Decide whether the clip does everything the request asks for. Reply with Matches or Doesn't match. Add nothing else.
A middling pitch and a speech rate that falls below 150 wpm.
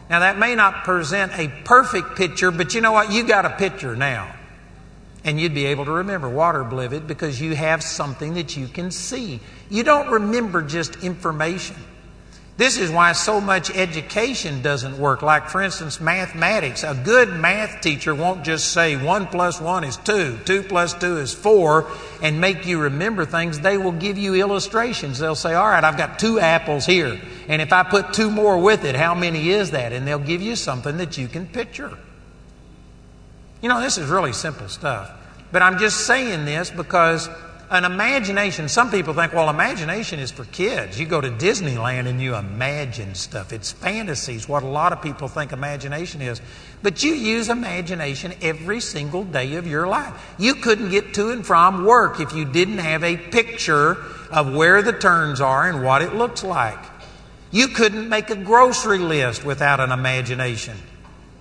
Doesn't match